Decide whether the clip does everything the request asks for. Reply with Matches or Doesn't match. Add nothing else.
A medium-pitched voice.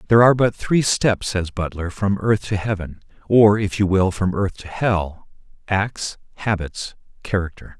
Doesn't match